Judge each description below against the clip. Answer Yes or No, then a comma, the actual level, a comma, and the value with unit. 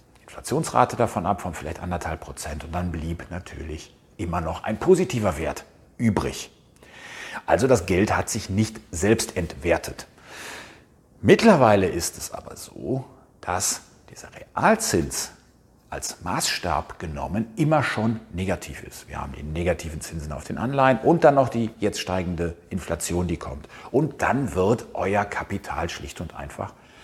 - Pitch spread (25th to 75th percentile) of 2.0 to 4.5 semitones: No, average, 5.3 semitones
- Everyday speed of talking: Yes, average, 145 wpm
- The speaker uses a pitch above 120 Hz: No, very low, 90 Hz